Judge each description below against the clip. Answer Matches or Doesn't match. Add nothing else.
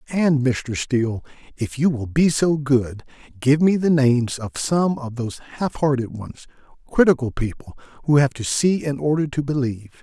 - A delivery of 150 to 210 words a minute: Matches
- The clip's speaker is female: Doesn't match